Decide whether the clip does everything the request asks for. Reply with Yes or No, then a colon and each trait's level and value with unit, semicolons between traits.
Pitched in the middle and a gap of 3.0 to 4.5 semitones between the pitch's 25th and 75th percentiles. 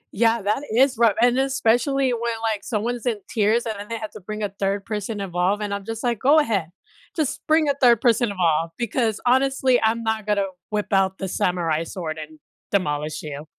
No: high, 215 Hz; average, 3.7 semitones